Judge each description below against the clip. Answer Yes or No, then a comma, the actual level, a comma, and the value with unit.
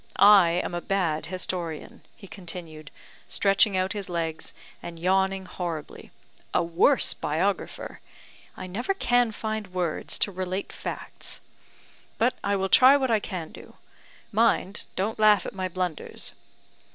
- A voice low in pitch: No, high, 190 Hz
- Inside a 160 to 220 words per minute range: No, average, 140 wpm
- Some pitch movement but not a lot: Yes, average, 3.3 semitones